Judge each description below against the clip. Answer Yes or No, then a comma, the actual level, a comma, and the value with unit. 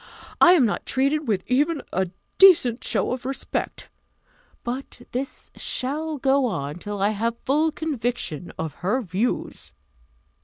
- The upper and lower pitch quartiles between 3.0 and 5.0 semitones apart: No, wide, 5.6 semitones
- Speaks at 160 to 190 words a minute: No, average, 140 wpm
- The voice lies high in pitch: Yes, very high, 250 Hz